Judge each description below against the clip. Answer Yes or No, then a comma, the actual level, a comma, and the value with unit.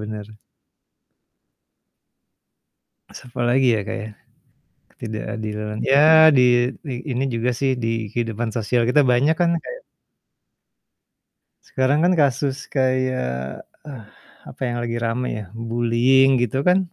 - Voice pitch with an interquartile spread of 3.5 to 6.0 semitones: No, average, 2.8 semitones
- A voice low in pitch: Yes, low, 125 Hz